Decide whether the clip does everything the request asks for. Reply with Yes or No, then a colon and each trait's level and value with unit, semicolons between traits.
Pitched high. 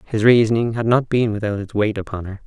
No: low, 110 Hz